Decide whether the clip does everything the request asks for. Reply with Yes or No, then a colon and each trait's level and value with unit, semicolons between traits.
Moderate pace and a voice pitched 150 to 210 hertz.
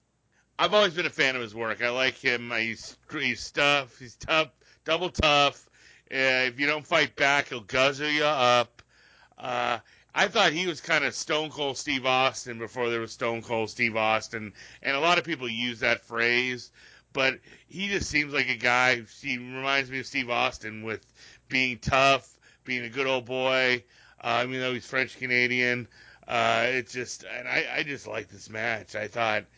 No: average, 190 wpm; low, 125 Hz